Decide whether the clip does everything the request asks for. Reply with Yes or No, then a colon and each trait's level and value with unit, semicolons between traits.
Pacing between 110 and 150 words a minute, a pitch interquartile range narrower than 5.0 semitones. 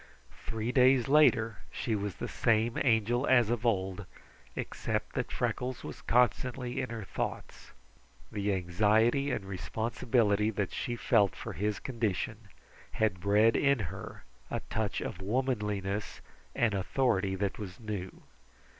Yes: slow, 135 wpm; average, 3.3 semitones